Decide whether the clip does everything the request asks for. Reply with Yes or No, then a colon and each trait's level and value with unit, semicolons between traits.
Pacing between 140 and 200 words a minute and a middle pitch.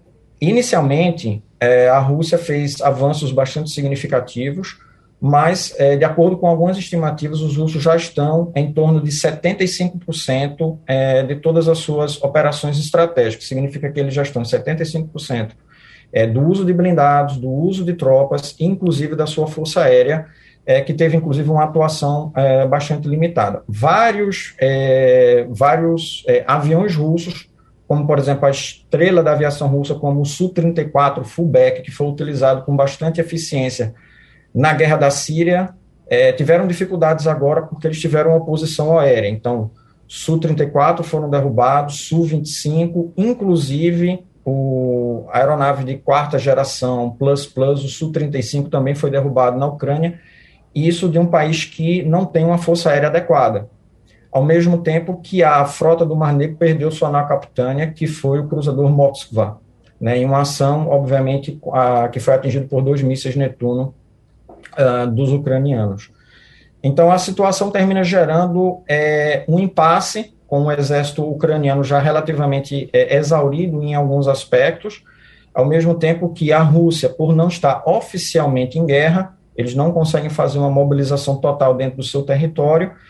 Yes: average, 145 wpm; medium, 150 Hz